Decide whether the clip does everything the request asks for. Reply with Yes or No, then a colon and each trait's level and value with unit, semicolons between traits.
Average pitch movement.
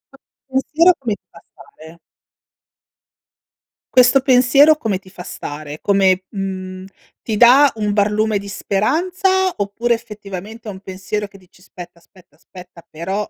Yes: average, 4.8 semitones